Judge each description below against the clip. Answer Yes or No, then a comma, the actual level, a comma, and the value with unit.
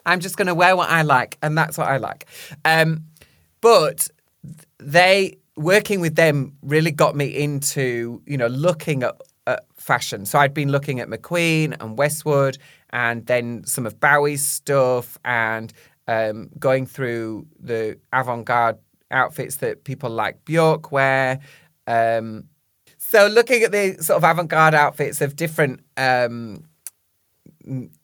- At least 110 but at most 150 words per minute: Yes, average, 145 wpm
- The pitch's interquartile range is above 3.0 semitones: Yes, average, 4.7 semitones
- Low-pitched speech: No, medium, 145 Hz